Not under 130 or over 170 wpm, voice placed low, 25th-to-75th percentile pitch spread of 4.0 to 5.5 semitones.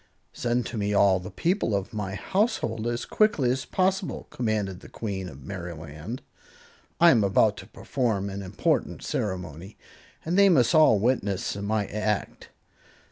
Yes: average, 150 wpm; low, 105 Hz; average, 4.5 semitones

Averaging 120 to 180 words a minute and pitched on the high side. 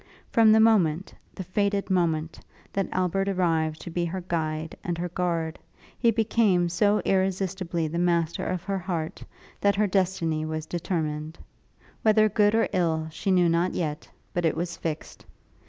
No: average, 160 wpm; medium, 175 Hz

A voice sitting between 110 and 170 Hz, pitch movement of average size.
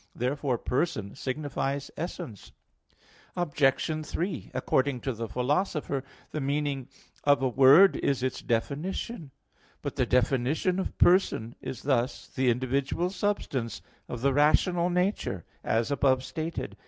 Yes: medium, 140 Hz; average, 3.9 semitones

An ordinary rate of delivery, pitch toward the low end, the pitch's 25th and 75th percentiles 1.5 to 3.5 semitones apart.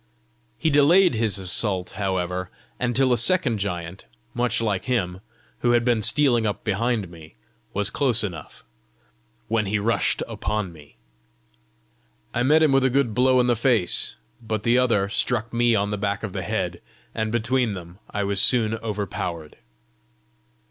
No: average, 160 wpm; low, 110 Hz; average, 3.9 semitones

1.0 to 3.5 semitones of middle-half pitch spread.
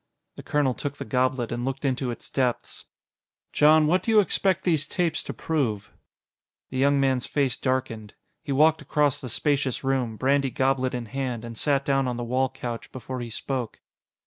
Yes: narrow, 2.5 semitones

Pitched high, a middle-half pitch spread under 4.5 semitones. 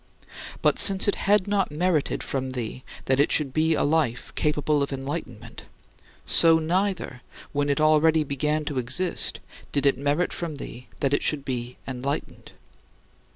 No: medium, 145 Hz; average, 3.3 semitones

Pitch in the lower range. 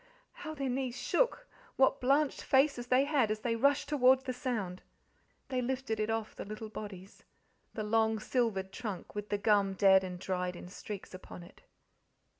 No: high, 225 Hz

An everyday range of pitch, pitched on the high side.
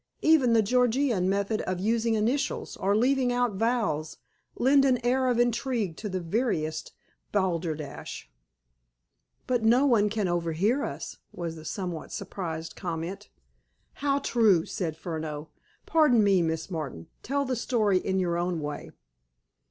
No: wide, 6.4 semitones; high, 205 Hz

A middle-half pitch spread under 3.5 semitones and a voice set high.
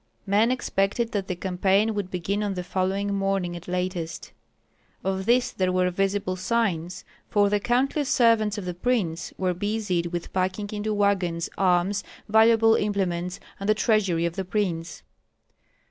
Yes: narrow, 2.6 semitones; high, 195 Hz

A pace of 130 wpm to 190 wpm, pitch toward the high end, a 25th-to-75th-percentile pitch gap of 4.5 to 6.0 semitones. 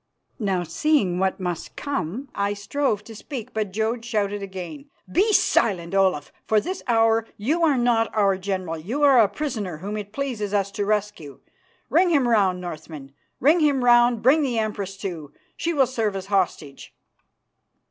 Yes: average, 170 wpm; high, 210 Hz; average, 4.9 semitones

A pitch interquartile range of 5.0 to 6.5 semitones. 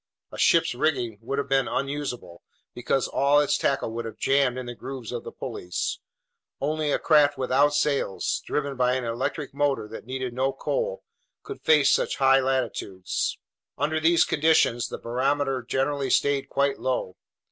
No: average, 2.8 semitones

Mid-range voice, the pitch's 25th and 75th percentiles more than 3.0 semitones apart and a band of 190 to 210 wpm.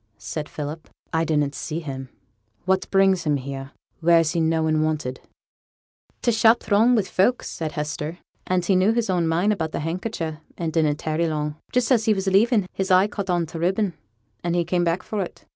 Yes: medium, 170 Hz; average, 3.7 semitones; average, 200 wpm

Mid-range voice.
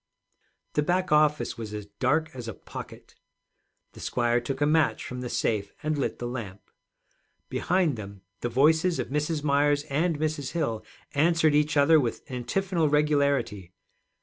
Yes: medium, 145 Hz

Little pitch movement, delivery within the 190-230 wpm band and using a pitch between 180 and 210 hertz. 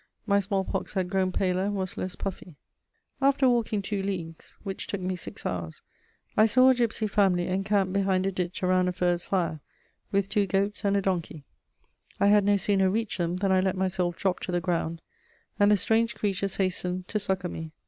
Yes: narrow, 2.0 semitones; average, 200 wpm; high, 190 Hz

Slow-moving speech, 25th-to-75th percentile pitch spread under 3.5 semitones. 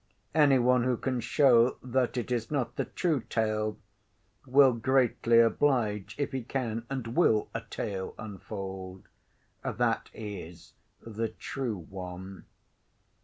No: slow, 125 wpm; average, 3.8 semitones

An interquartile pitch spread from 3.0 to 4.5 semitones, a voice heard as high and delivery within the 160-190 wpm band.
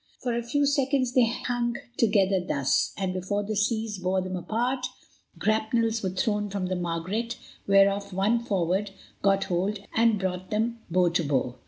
Yes: average, 3.8 semitones; high, 205 Hz; average, 165 wpm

